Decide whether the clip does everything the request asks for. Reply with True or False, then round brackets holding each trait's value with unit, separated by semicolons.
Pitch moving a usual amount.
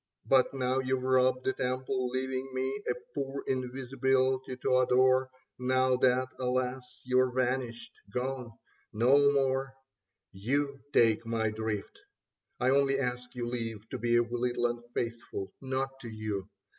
False (1.6 semitones)